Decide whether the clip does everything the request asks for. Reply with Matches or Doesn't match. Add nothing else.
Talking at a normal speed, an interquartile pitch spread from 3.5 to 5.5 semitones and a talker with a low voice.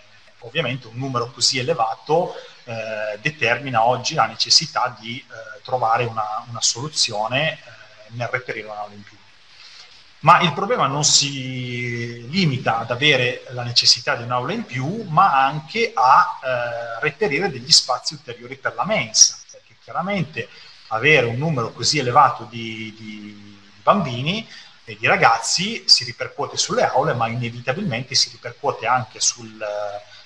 Matches